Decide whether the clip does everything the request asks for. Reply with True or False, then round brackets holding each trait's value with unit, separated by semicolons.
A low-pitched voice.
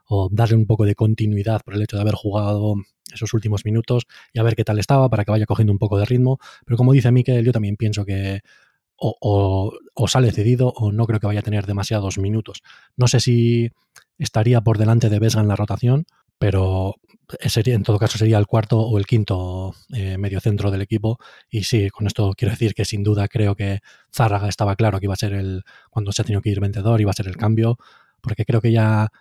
True (110 Hz)